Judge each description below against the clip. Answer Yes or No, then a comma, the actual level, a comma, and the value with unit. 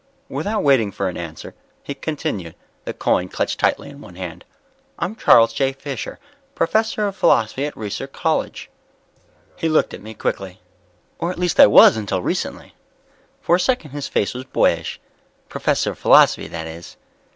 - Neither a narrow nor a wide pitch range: No, wide, 8.7 semitones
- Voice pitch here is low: Yes, low, 130 Hz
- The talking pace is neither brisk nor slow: Yes, average, 165 wpm